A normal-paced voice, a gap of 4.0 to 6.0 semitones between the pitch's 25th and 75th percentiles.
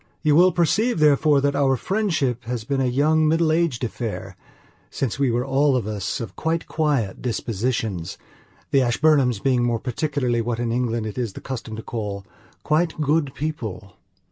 Yes: average, 170 wpm; average, 4.7 semitones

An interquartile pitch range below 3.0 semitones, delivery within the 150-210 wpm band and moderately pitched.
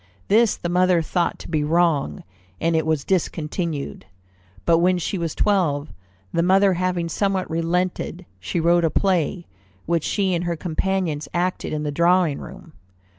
Yes: narrow, 2.4 semitones; average, 160 wpm; medium, 170 Hz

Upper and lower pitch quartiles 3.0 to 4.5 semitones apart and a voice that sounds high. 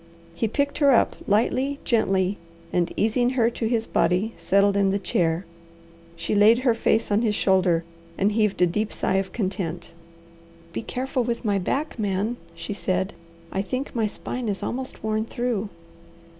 Yes: average, 3.7 semitones; high, 215 Hz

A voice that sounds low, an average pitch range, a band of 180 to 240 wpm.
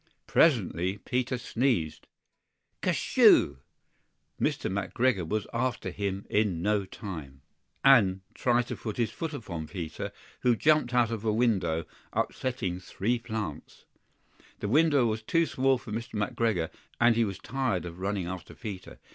No: low, 110 Hz; average, 4.7 semitones; average, 140 wpm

